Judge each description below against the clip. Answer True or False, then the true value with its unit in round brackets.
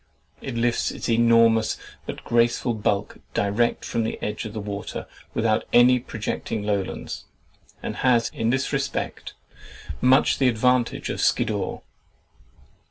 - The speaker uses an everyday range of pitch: False (2.0 semitones)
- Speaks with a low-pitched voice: True (115 Hz)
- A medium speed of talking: False (130 wpm)